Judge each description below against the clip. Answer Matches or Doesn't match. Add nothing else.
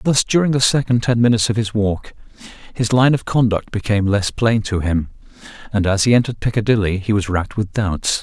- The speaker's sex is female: Doesn't match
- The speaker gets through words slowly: Doesn't match